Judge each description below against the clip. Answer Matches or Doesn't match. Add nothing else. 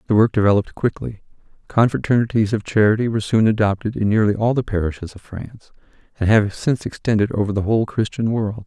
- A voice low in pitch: Matches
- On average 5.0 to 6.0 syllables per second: Doesn't match